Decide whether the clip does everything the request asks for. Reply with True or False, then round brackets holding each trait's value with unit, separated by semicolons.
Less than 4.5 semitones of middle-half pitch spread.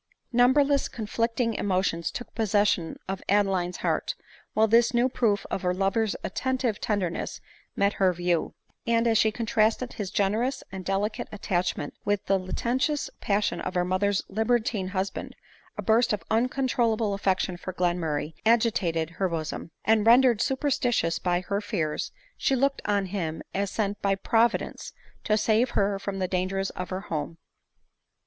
True (3.8 semitones)